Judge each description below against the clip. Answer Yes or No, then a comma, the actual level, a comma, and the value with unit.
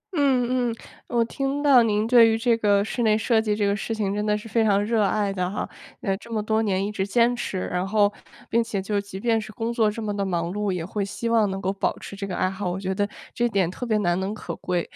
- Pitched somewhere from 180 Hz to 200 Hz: No, high, 210 Hz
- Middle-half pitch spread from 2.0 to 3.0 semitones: Yes, average, 2.7 semitones